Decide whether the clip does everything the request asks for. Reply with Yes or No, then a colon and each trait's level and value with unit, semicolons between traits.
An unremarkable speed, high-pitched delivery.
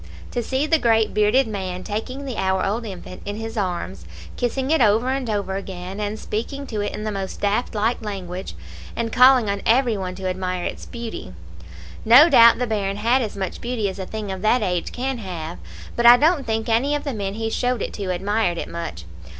No: fast, 215 wpm; high, 215 Hz